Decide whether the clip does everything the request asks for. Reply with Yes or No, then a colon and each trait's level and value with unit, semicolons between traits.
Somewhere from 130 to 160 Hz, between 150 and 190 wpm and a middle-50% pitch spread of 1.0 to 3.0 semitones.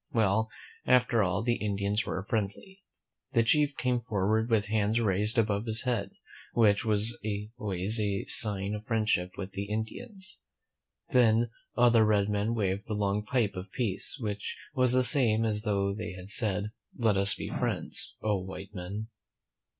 No: low, 105 Hz; average, 160 wpm; narrow, 2.5 semitones